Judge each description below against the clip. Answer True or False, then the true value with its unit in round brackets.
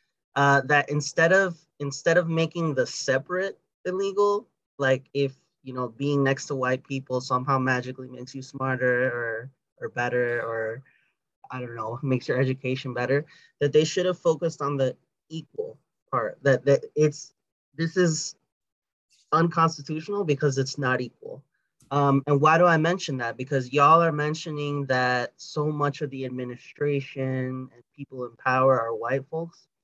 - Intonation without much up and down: False (3.6 semitones)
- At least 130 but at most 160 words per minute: True (155 wpm)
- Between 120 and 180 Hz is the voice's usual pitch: True (140 Hz)